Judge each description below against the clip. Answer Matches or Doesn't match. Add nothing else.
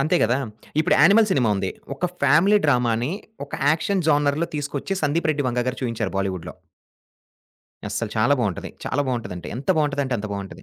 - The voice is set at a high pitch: Doesn't match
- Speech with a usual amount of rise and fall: Matches